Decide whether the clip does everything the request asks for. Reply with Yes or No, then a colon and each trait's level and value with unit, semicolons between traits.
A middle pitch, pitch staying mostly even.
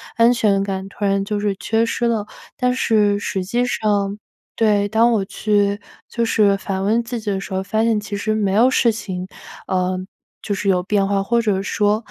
No: high, 205 Hz; narrow, 2.2 semitones